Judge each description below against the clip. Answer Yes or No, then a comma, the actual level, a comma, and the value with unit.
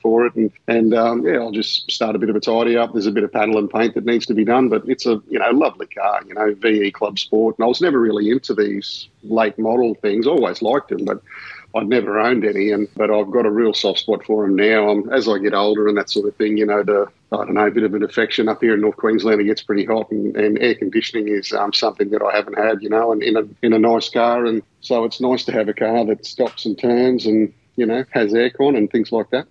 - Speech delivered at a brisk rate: Yes, fast, 285 wpm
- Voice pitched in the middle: No, low, 110 Hz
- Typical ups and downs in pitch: No, narrow, 1.7 semitones